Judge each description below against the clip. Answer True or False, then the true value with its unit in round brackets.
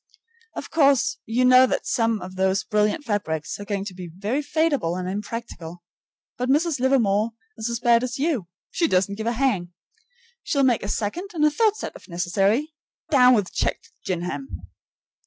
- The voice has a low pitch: False (225 Hz)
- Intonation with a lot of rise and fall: True (6.0 semitones)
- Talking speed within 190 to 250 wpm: False (175 wpm)